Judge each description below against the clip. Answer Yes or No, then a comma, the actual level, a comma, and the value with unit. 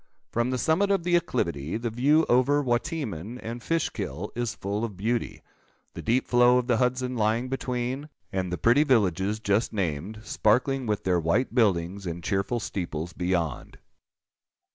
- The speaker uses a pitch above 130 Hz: No, low, 115 Hz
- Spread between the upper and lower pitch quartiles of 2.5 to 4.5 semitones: No, average, 4.9 semitones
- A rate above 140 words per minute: Yes, average, 160 wpm